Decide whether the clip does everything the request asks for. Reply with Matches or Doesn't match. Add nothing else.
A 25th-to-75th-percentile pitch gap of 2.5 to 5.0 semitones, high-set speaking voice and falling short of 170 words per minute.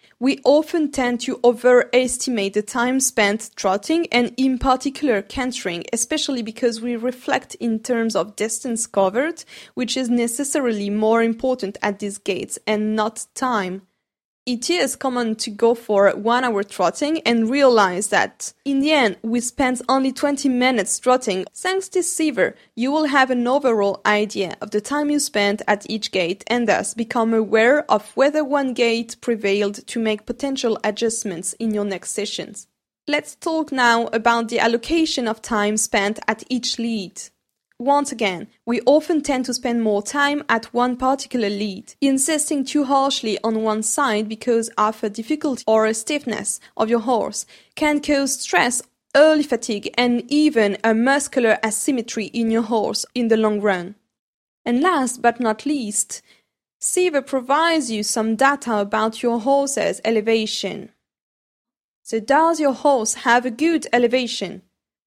Matches